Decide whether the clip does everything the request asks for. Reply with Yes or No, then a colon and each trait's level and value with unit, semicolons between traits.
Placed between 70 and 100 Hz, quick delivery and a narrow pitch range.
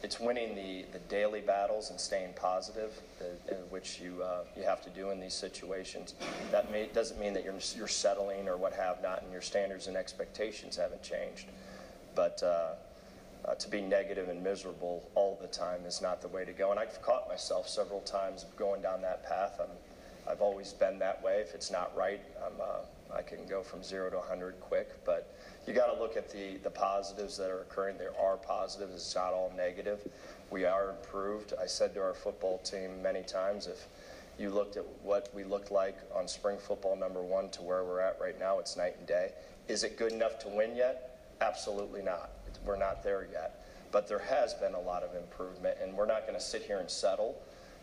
Yes: very low, 95 Hz; fast, 215 wpm; narrow, 1.9 semitones